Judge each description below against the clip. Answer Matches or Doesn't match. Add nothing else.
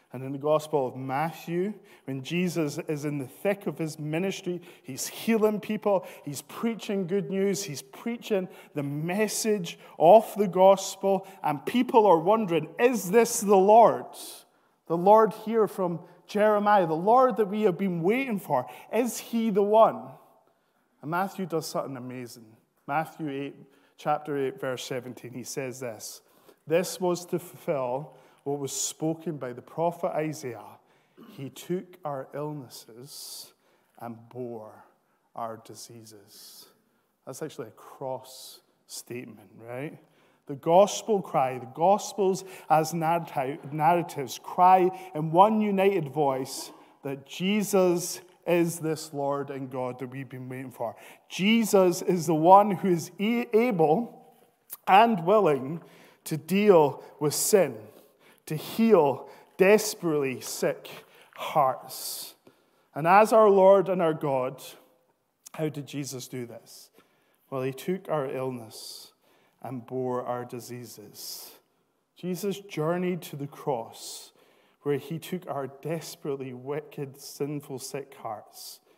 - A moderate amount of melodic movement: Doesn't match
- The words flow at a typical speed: Doesn't match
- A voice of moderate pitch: Matches